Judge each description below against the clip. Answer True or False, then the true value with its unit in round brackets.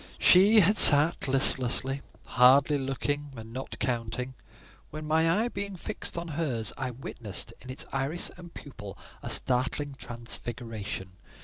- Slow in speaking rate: True (125 wpm)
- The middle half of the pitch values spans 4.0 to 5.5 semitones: True (4.7 semitones)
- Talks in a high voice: False (135 Hz)